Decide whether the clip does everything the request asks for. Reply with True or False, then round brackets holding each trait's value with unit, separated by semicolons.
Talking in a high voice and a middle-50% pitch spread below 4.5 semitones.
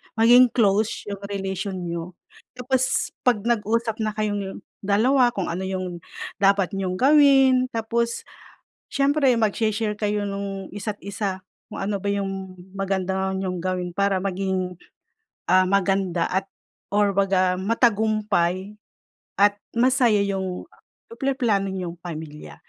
True (200 Hz; 2.8 semitones)